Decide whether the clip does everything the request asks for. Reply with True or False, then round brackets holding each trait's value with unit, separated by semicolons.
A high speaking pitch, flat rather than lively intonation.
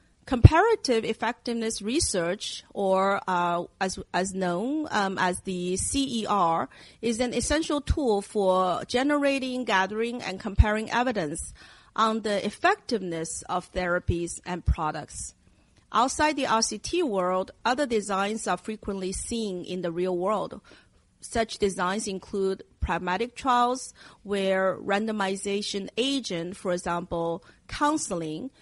False (200 Hz; 4.5 semitones)